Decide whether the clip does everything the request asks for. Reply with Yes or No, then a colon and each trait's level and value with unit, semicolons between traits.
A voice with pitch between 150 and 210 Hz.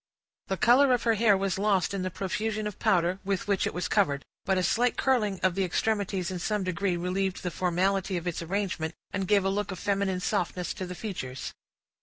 Yes: high, 190 Hz